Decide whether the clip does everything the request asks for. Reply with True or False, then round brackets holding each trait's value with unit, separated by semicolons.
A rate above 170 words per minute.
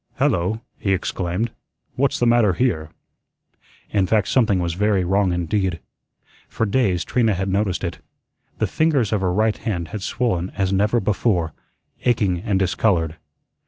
False (150 wpm)